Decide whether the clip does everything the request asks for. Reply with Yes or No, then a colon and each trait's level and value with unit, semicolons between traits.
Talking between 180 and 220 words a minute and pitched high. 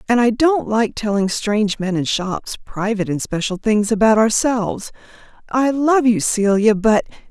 No: average, 165 wpm; high, 220 Hz